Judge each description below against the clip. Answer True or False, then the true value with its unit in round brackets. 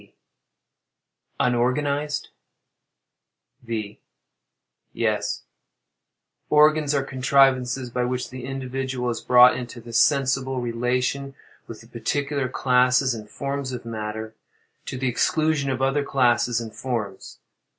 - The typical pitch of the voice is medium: False (125 Hz)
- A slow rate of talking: True (105 wpm)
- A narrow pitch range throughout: True (2.3 semitones)